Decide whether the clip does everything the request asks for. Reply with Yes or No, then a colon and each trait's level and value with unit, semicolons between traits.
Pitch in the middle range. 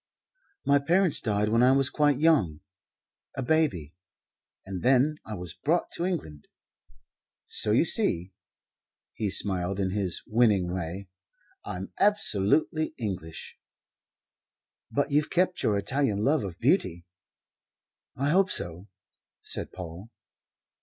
No: low, 110 Hz